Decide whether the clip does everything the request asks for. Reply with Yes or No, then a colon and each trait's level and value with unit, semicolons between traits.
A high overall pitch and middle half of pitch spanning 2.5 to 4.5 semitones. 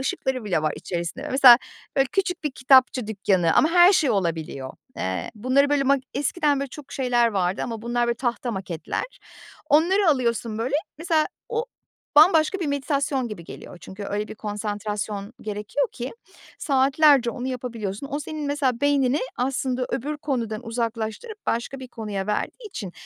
No: very high, 250 Hz; average, 5.2 semitones